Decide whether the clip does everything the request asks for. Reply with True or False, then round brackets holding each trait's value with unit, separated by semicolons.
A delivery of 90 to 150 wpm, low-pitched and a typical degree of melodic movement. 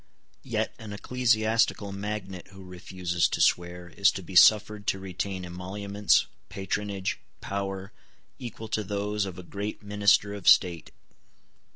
False (135 wpm; 100 Hz; 2.0 semitones)